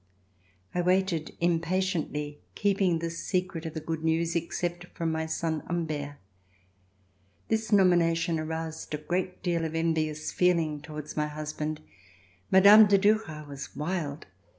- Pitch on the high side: No, medium, 165 Hz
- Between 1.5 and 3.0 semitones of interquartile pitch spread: Yes, narrow, 2.6 semitones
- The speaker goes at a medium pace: No, slow, 130 wpm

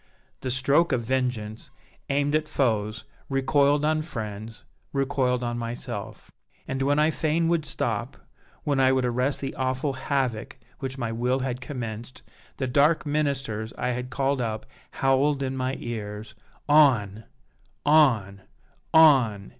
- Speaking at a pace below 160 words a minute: Yes, average, 140 wpm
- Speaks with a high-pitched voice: No, low, 130 Hz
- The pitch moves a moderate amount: Yes, average, 3.4 semitones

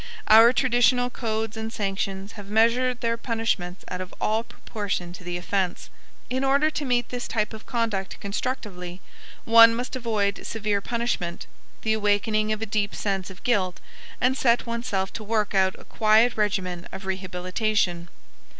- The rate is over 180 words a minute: No, average, 160 wpm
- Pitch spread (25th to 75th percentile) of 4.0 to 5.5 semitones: No, average, 3.3 semitones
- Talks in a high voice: Yes, high, 215 Hz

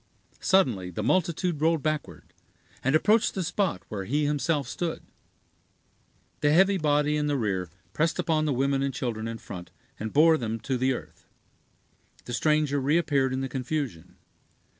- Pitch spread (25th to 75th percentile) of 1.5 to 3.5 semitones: No, average, 4.3 semitones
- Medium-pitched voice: Yes, medium, 145 Hz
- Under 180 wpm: Yes, average, 160 wpm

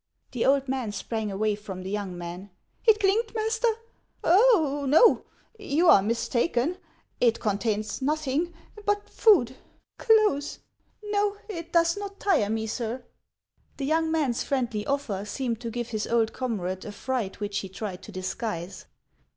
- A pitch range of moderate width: No, wide, 8.1 semitones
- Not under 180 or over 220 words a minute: No, average, 155 wpm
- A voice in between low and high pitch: No, very high, 250 Hz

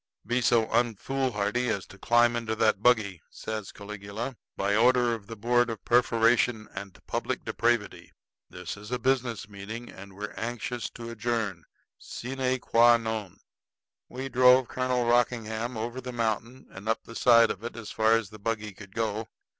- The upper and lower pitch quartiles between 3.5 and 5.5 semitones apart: No, narrow, 2.4 semitones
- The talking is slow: No, average, 165 wpm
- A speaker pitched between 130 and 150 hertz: No, low, 115 Hz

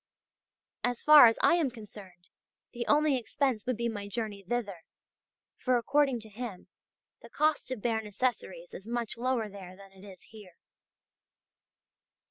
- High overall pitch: Yes, high, 230 Hz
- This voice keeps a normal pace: Yes, average, 150 wpm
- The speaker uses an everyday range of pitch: Yes, average, 4.0 semitones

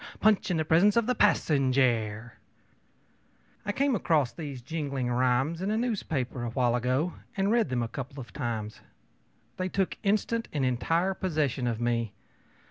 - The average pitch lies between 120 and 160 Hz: Yes, medium, 140 Hz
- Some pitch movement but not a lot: No, wide, 7.5 semitones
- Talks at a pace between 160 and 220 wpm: Yes, average, 165 wpm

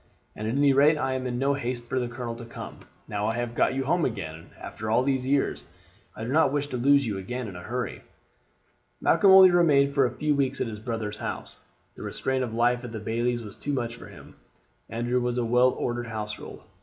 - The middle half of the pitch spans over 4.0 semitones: No, average, 3.0 semitones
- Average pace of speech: No, fast, 230 wpm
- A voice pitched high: No, low, 125 Hz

